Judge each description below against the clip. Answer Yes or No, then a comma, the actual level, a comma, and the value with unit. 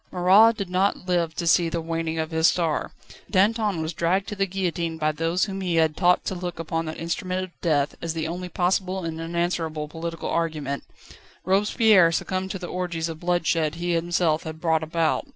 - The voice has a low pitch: No, medium, 170 Hz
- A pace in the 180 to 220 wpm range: Yes, average, 195 wpm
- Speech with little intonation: Yes, narrow, 2.2 semitones